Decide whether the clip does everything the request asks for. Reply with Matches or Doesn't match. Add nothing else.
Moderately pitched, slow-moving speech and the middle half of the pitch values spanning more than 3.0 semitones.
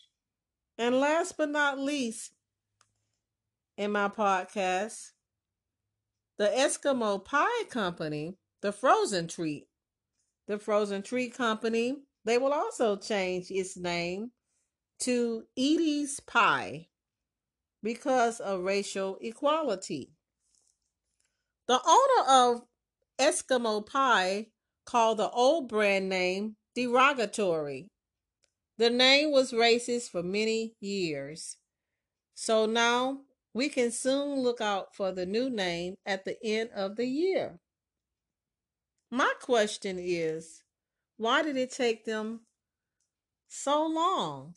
Doesn't match